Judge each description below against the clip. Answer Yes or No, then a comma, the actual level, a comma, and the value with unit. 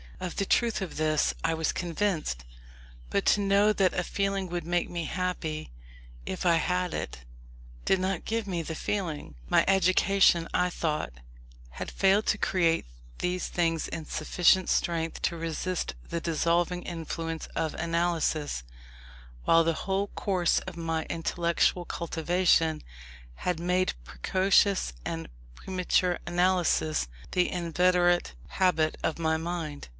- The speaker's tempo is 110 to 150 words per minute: Yes, slow, 135 wpm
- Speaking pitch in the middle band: Yes, medium, 175 Hz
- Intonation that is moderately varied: No, narrow, 2.2 semitones